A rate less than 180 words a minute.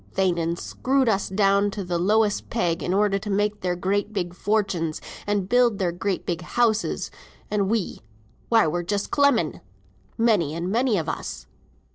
Yes: average, 165 wpm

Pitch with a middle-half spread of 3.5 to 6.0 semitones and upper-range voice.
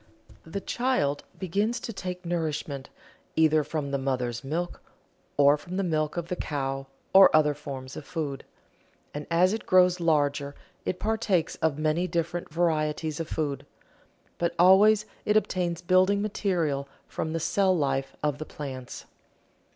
No: average, 4.2 semitones; medium, 160 Hz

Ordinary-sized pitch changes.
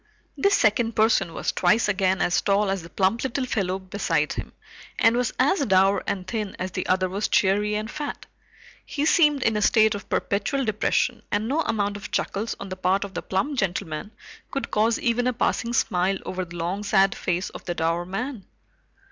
Yes: average, 3.6 semitones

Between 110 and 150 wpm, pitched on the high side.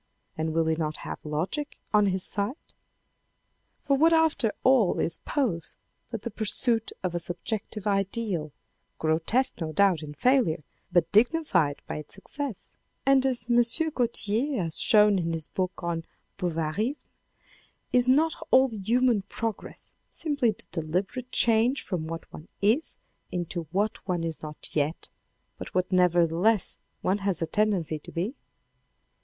Yes: average, 145 wpm; high, 200 Hz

